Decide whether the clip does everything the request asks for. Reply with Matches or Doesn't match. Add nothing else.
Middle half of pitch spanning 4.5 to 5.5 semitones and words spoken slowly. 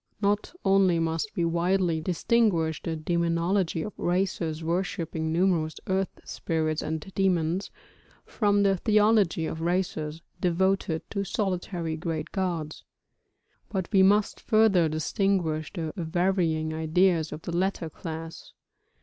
Doesn't match